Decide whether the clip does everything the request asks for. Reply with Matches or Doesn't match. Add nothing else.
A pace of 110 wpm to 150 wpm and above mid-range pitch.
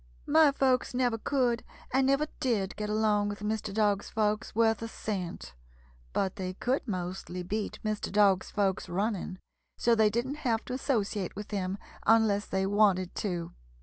Doesn't match